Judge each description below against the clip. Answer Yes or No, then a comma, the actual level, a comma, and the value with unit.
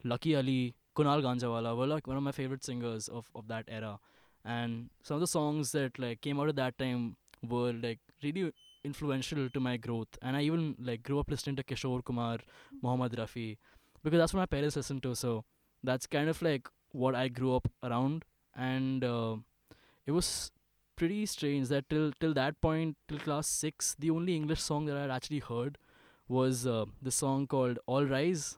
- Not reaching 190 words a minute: No, average, 195 wpm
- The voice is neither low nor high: No, low, 130 Hz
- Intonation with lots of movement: No, average, 3.5 semitones